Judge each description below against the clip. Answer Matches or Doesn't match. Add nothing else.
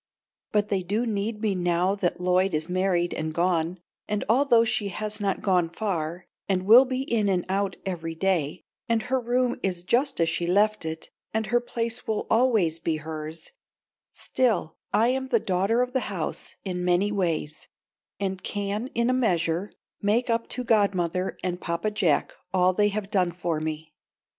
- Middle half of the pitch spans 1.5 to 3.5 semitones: Doesn't match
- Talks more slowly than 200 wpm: Matches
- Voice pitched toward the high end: Matches